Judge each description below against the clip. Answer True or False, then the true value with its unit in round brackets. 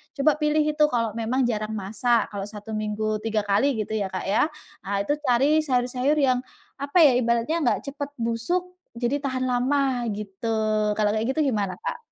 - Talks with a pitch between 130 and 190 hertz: False (240 Hz)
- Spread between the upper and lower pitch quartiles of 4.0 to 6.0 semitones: True (4.7 semitones)